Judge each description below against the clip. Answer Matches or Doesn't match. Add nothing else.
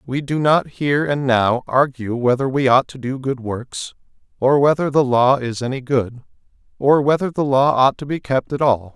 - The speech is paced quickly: Matches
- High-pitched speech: Doesn't match